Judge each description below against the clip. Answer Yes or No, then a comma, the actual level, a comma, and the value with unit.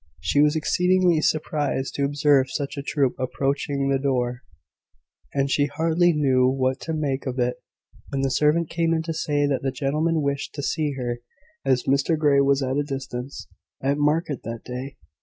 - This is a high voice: No, medium, 140 Hz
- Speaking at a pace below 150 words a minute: No, average, 180 wpm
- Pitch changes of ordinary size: No, narrow, 2.3 semitones